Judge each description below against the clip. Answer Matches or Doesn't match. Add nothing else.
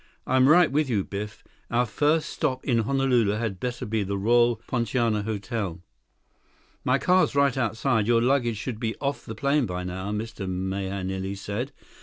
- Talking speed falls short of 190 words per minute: Matches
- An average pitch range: Matches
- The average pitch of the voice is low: Matches